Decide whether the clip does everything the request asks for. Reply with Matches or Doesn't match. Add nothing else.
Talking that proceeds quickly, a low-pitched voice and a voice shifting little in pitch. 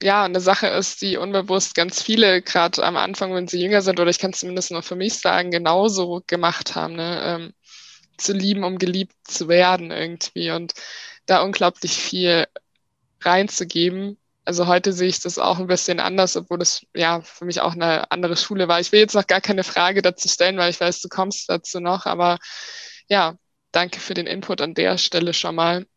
Doesn't match